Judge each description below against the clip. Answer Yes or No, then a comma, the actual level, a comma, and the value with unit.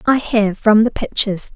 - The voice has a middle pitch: No, high, 215 Hz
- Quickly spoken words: No, average, 190 wpm